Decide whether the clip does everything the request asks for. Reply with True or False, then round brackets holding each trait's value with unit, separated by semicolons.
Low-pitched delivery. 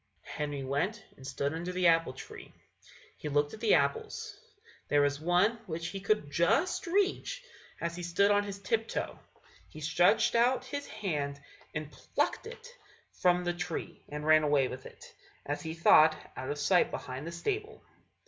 False (170 Hz)